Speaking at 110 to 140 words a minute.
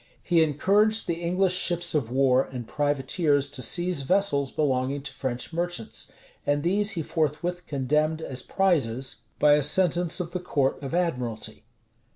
No: average, 160 wpm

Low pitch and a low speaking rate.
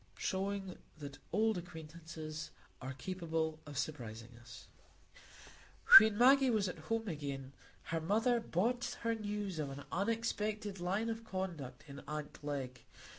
No: medium, 175 Hz; slow, 130 wpm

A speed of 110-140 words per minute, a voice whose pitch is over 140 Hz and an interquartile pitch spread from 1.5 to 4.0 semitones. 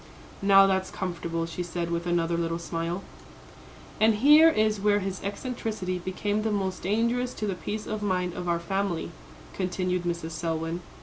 No: average, 165 wpm; medium, 185 Hz; average, 3.4 semitones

